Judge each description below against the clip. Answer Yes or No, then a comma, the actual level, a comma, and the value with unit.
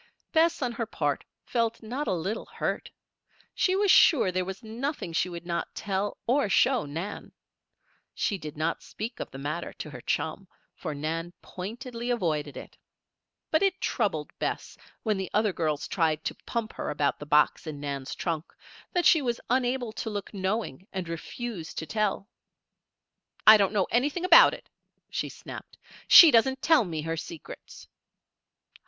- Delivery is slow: No, average, 165 wpm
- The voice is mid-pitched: No, high, 200 Hz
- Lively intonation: Yes, wide, 6.8 semitones